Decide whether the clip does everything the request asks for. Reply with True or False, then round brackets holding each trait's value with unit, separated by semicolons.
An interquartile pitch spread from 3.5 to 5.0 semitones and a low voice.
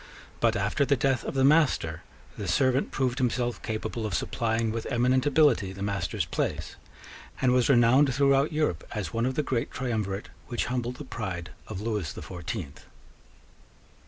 True (4.3 semitones; 120 Hz)